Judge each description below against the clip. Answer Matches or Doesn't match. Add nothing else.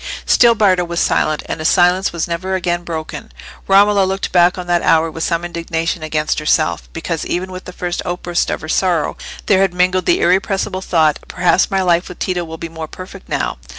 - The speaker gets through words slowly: Doesn't match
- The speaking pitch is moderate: Matches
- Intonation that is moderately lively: Doesn't match